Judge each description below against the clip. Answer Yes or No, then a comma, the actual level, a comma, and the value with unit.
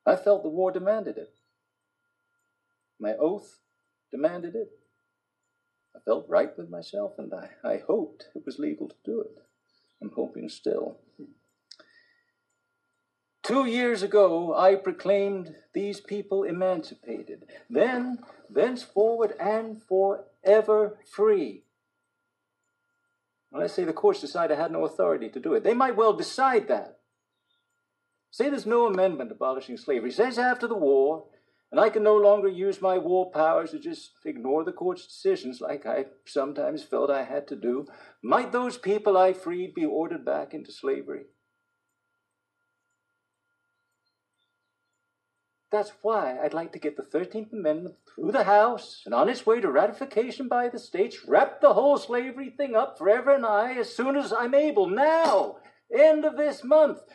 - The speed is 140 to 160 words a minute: Yes, average, 150 wpm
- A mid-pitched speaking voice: No, high, 205 Hz